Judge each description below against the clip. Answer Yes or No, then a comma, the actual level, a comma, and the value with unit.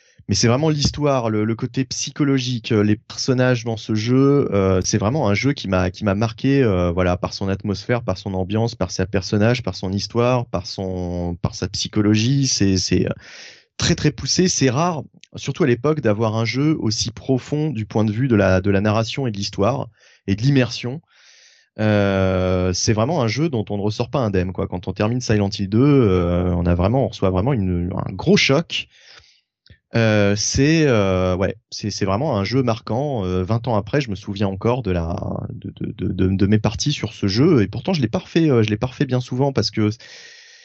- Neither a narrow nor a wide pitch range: Yes, average, 4.7 semitones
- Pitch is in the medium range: No, low, 110 Hz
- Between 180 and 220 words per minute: Yes, average, 210 wpm